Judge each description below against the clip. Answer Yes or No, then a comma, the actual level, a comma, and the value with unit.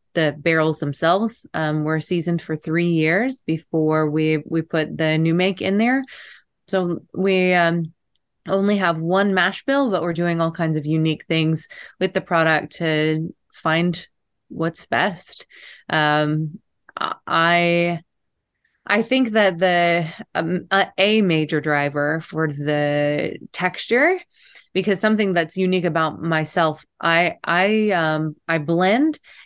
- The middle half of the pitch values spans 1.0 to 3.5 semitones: Yes, average, 3.1 semitones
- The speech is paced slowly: Yes, slow, 130 wpm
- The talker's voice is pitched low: No, medium, 170 Hz